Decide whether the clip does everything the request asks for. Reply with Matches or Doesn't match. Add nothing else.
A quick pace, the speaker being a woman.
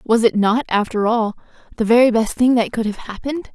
Matches